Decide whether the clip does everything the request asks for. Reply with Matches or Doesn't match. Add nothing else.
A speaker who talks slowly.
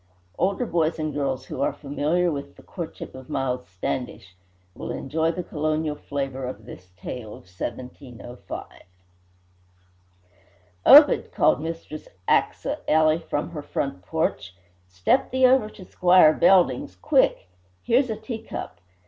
Matches